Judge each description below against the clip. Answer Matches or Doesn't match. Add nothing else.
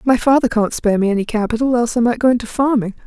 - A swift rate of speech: Matches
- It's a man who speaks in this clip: Doesn't match